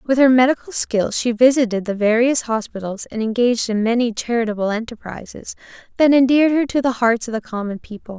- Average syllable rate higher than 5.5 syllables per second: Yes, 5.8 syllables/s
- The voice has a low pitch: No, high, 235 Hz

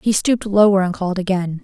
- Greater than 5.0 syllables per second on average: Yes, 6.5 syllables/s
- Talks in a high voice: Yes, high, 195 Hz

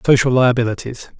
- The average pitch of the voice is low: Yes, low, 120 Hz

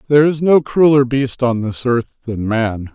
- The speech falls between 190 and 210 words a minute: Yes, fast, 205 wpm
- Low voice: Yes, low, 125 Hz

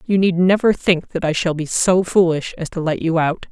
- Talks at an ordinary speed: No, fast, 255 wpm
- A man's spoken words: No, female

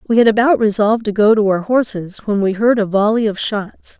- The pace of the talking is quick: Yes, fast, 240 wpm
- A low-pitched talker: No, high, 215 Hz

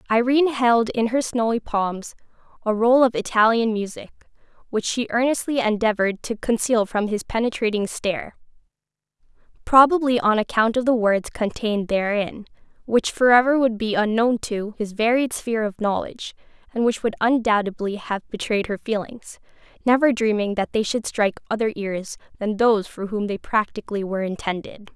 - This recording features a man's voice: No, female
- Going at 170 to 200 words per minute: No, average, 155 wpm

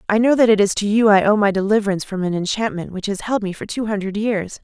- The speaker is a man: No, female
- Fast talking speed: Yes, fast, 285 wpm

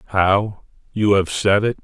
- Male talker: Yes, male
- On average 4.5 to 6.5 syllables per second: No, 4.0 syllables/s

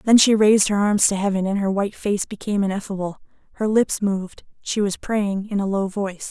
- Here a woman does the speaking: Yes, female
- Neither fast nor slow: No, fast, 220 wpm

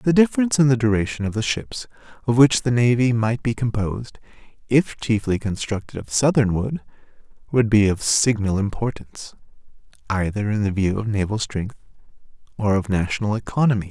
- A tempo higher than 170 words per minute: No, average, 160 wpm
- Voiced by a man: Yes, male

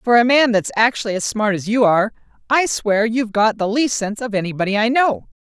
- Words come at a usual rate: No, fast, 230 wpm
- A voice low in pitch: No, high, 225 Hz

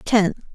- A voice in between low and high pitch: No, high, 205 Hz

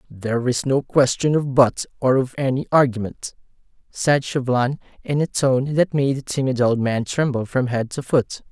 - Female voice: No, male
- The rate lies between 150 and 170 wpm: No, average, 185 wpm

